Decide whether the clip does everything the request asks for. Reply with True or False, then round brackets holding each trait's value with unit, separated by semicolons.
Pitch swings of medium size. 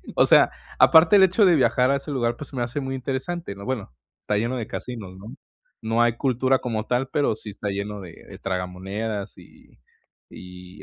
True (4.9 semitones)